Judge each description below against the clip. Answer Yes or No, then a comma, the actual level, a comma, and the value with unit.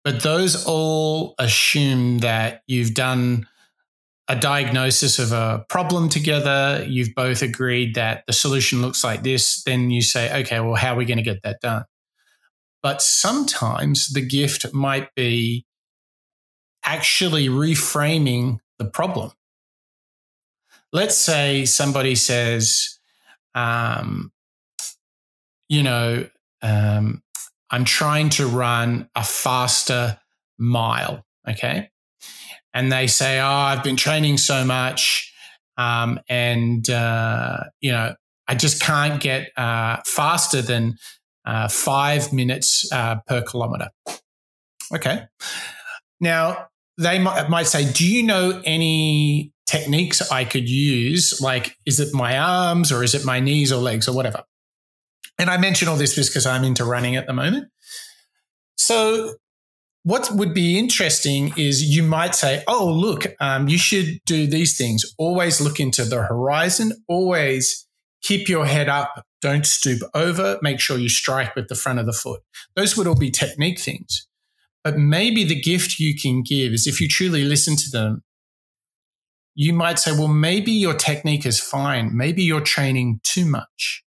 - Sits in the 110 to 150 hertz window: Yes, medium, 140 Hz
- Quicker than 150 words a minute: No, average, 145 wpm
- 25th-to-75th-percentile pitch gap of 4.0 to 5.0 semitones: Yes, average, 4.4 semitones